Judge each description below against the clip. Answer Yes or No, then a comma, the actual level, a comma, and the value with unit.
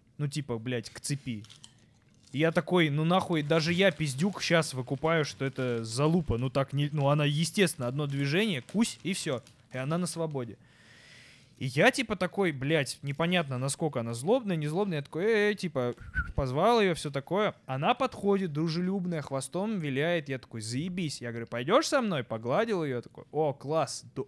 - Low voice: No, medium, 150 Hz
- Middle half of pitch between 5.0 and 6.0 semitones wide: Yes, wide, 5.4 semitones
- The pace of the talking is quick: Yes, fast, 175 wpm